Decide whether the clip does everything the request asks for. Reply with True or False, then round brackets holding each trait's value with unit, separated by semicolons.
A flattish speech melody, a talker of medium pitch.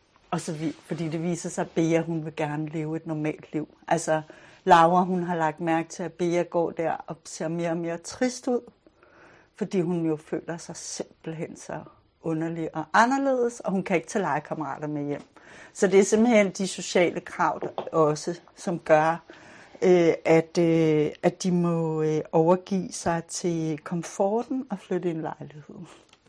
True (2.3 semitones; 170 Hz)